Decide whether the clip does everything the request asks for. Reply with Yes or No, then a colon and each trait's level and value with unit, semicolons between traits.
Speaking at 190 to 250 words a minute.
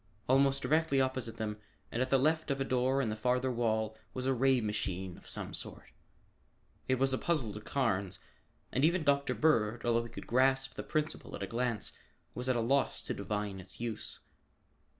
Yes: average, 195 wpm